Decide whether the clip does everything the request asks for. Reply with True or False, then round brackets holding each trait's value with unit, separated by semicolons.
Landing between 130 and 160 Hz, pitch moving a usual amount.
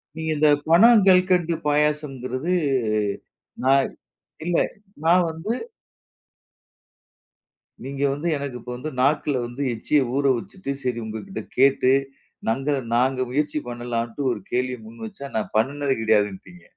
True (140 Hz; 4.2 semitones)